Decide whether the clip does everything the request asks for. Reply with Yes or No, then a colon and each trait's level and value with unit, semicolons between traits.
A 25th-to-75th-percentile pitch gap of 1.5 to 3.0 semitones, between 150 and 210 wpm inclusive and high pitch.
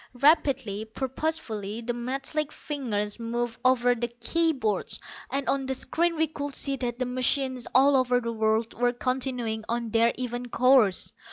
Yes: average, 2.7 semitones; average, 160 wpm; very high, 250 Hz